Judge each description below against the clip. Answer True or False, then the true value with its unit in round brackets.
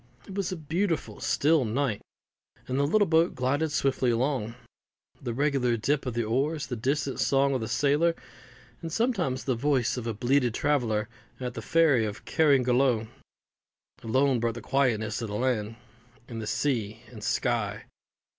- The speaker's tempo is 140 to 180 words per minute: True (160 wpm)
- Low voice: True (130 Hz)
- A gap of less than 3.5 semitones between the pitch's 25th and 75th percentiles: False (3.9 semitones)